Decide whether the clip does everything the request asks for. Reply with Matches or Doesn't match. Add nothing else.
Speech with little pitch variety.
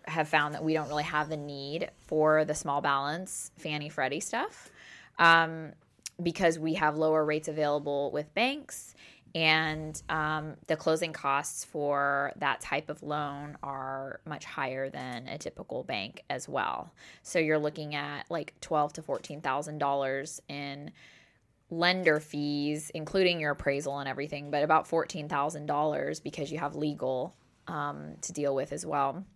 Matches